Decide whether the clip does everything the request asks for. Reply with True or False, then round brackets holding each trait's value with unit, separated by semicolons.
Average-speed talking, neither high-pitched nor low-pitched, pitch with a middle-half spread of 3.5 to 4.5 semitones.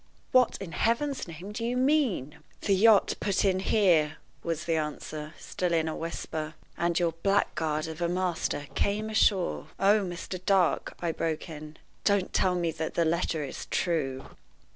True (170 wpm; 175 Hz; 3.9 semitones)